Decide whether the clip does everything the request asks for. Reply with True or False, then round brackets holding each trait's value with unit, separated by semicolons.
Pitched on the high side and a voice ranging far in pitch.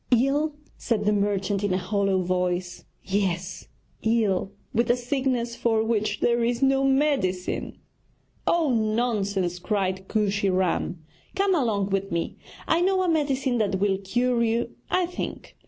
False (215 Hz; 4.5 semitones)